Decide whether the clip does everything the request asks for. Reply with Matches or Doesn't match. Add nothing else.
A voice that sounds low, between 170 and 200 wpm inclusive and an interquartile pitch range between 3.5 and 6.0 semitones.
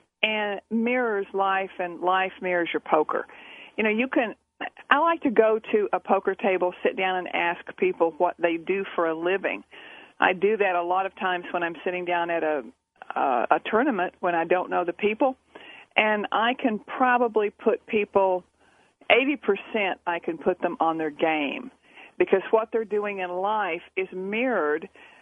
Doesn't match